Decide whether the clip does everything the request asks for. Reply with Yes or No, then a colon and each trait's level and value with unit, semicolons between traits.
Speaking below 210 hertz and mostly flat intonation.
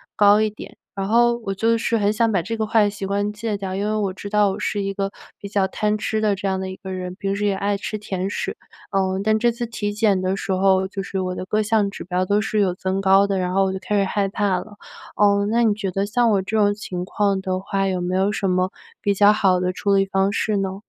Yes: high, 200 Hz; narrow, 1.7 semitones